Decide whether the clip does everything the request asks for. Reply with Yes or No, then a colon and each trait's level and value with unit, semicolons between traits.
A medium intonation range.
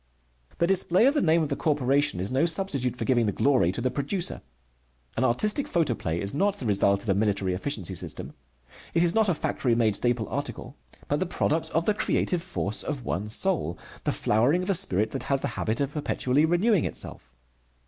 No: wide, 7.7 semitones